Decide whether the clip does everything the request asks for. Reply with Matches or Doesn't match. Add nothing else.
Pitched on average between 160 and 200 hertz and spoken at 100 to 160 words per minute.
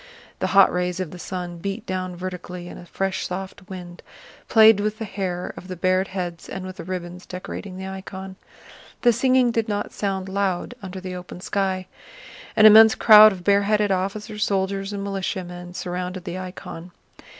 Doesn't match